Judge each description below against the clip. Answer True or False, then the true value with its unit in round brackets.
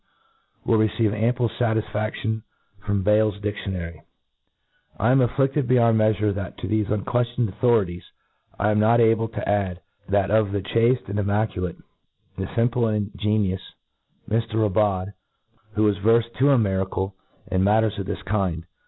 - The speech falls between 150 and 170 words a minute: True (155 wpm)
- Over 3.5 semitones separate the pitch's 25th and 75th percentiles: False (2.4 semitones)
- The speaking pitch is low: True (105 Hz)